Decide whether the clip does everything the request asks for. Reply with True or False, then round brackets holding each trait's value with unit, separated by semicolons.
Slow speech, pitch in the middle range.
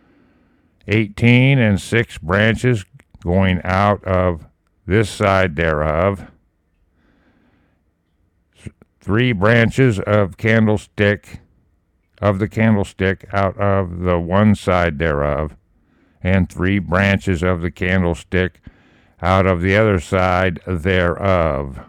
False (95 wpm; 95 Hz)